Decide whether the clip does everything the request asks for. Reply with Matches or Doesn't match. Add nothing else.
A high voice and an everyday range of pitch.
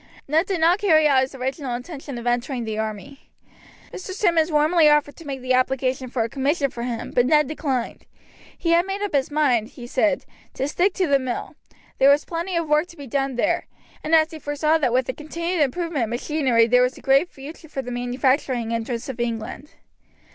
Matches